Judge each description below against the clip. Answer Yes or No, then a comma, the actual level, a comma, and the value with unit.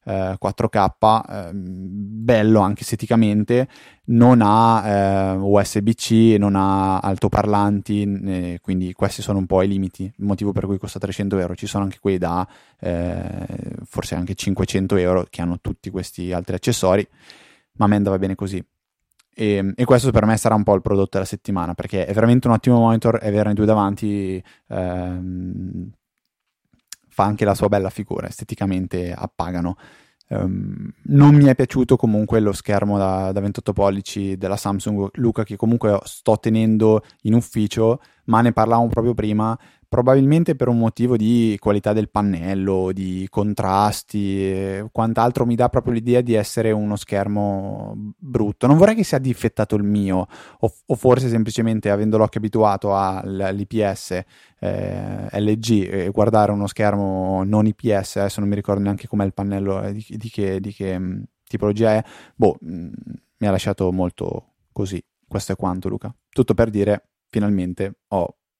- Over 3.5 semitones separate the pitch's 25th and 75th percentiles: No, narrow, 2.6 semitones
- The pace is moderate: Yes, average, 155 wpm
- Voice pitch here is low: Yes, low, 105 Hz